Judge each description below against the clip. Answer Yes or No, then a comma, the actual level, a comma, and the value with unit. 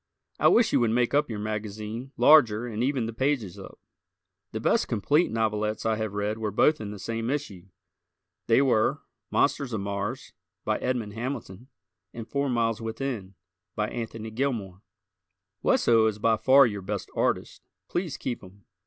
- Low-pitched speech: Yes, low, 115 Hz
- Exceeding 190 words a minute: No, average, 165 wpm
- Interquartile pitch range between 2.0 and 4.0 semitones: Yes, average, 3.4 semitones